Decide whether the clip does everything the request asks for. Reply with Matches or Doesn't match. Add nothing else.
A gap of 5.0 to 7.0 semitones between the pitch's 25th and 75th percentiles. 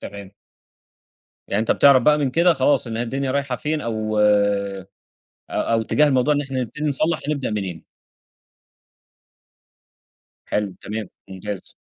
Matches